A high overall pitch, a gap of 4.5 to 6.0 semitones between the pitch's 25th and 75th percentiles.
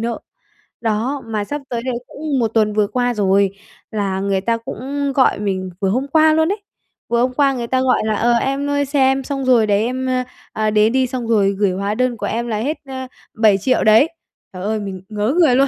No: high, 235 Hz; average, 4.0 semitones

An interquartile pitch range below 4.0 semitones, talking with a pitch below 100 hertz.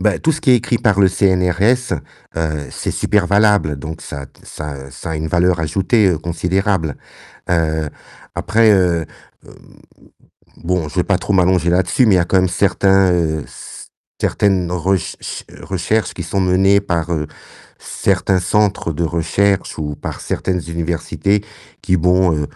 Yes: average, 3.3 semitones; very low, 90 Hz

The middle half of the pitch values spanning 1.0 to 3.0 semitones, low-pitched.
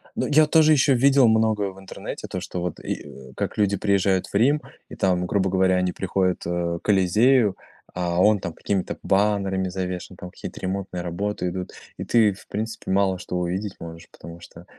Yes: average, 2.7 semitones; very low, 95 Hz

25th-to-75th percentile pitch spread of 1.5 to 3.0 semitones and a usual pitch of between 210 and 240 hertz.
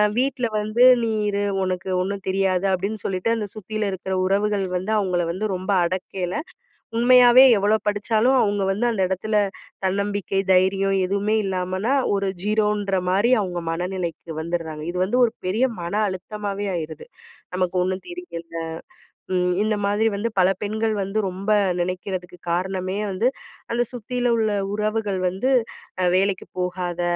No: average, 2.7 semitones; high, 195 Hz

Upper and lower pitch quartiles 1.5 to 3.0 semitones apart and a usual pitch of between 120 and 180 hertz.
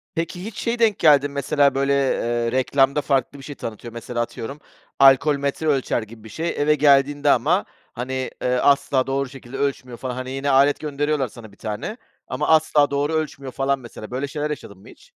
Yes: narrow, 2.5 semitones; medium, 140 Hz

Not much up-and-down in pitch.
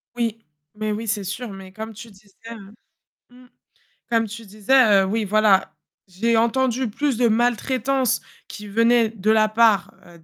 Yes: narrow, 2.2 semitones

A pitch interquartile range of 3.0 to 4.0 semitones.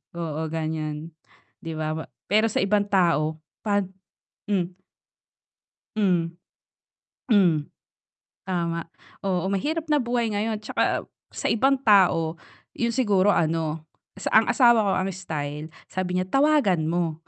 No: average, 4.7 semitones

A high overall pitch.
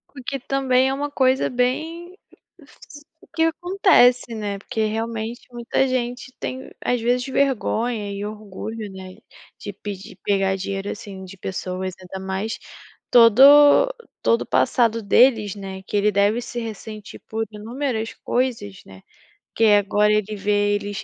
Yes: high, 225 Hz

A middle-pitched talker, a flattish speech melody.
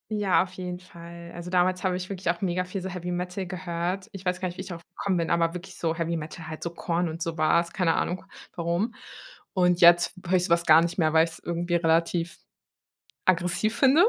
Yes: medium, 175 Hz; narrow, 1.5 semitones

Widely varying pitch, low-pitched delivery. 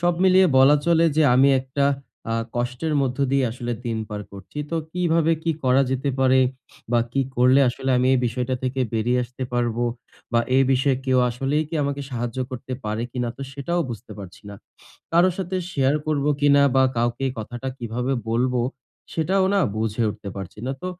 No: average, 3.1 semitones; low, 130 Hz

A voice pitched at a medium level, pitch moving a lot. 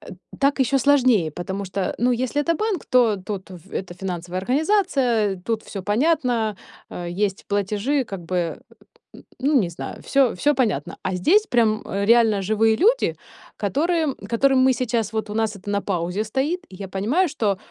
No: high, 220 Hz; wide, 5.7 semitones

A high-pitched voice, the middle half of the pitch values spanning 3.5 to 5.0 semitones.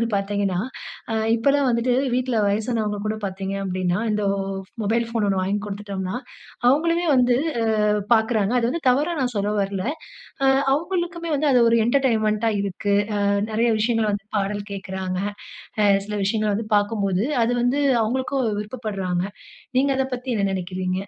Yes: high, 215 Hz; average, 3.8 semitones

